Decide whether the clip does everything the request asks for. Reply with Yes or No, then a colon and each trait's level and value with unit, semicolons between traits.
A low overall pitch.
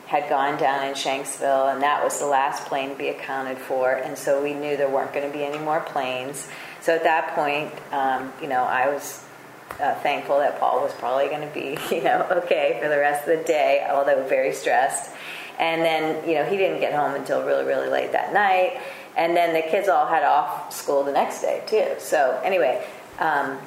No: medium, 145 Hz